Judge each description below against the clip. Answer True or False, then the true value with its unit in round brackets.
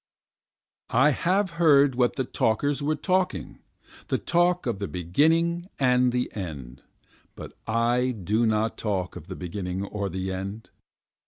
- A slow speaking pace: False (150 wpm)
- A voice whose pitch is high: False (120 Hz)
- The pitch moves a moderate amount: False (7.1 semitones)